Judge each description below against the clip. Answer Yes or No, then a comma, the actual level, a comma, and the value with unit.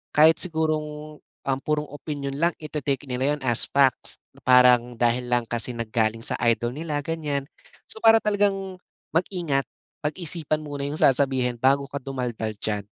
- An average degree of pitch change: Yes, average, 3.8 semitones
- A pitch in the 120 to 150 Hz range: Yes, medium, 140 Hz